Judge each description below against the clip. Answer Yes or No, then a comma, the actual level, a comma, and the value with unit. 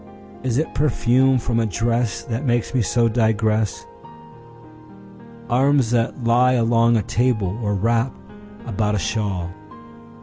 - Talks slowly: Yes, slow, 115 wpm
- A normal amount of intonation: No, narrow, 2.3 semitones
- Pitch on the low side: Yes, low, 115 Hz